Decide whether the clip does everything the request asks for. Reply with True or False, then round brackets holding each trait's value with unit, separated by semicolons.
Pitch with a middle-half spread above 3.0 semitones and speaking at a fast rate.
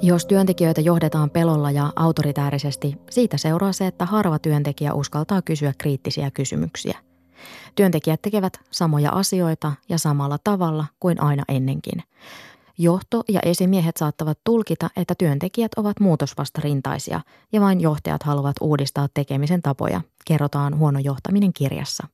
False (3.8 semitones; 125 wpm)